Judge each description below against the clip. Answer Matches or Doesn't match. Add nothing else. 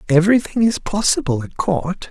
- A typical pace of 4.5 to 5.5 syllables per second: Matches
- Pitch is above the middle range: Doesn't match